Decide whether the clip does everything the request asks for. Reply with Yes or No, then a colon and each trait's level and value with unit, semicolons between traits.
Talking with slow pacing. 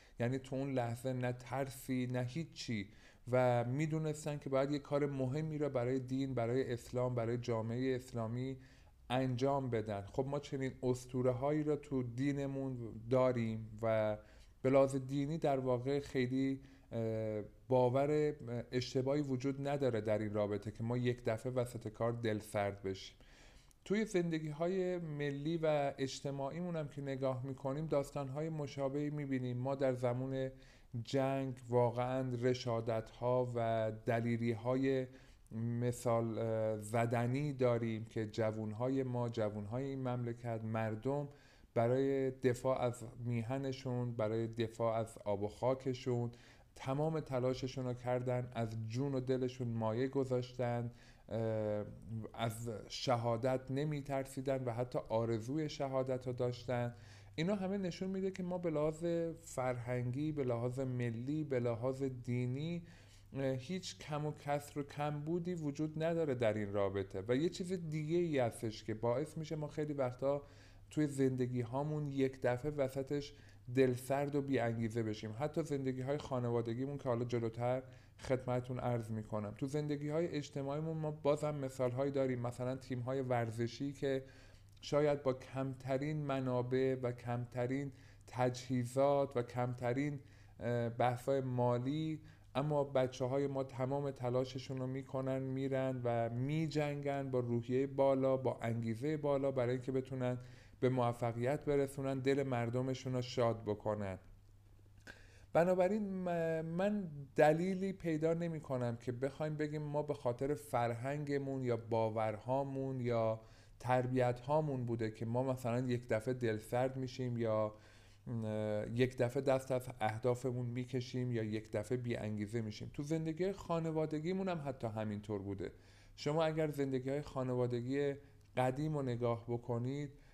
No: average, 135 wpm